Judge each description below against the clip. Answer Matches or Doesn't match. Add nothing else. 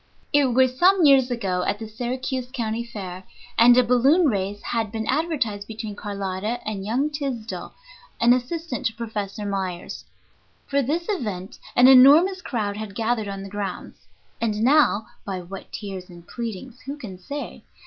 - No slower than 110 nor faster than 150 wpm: Doesn't match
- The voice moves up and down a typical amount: Matches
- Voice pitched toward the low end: Doesn't match